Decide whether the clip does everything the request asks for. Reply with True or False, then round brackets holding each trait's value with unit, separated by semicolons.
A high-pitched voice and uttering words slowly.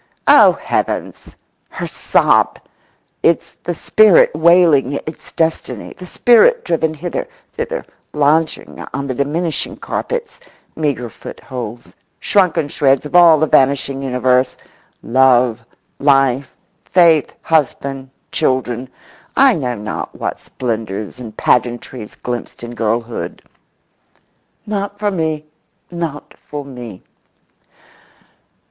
False (140 Hz; 95 wpm)